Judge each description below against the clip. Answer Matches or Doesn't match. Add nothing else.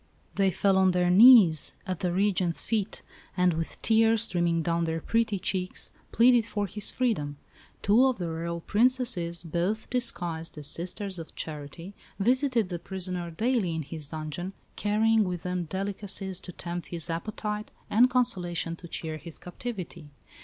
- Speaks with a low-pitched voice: Doesn't match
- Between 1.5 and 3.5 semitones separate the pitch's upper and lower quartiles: Doesn't match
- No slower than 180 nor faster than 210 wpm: Doesn't match